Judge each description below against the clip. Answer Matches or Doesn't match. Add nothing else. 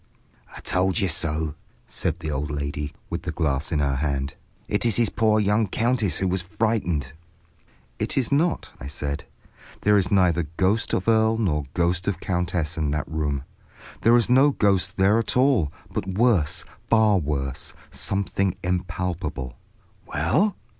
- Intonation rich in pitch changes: Matches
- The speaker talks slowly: Doesn't match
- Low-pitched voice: Matches